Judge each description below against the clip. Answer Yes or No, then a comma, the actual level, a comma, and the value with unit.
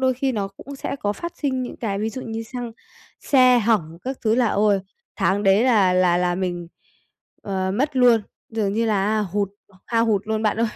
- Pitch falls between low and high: No, high, 220 Hz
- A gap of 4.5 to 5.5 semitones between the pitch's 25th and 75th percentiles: No, average, 3.9 semitones